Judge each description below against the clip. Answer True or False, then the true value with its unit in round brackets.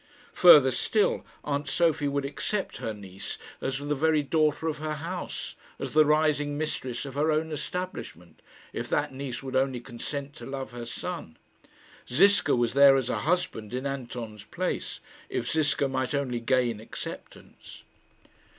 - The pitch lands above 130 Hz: True (140 Hz)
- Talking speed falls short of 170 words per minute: True (155 wpm)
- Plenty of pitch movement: False (3.6 semitones)